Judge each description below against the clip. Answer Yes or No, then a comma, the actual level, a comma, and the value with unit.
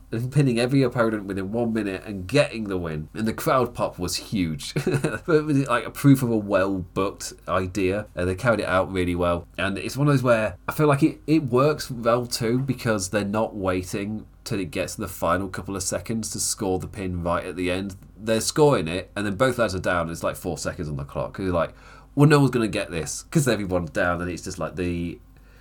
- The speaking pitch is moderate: No, low, 105 Hz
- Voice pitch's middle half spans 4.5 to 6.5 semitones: Yes, average, 4.9 semitones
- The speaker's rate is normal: No, fast, 240 wpm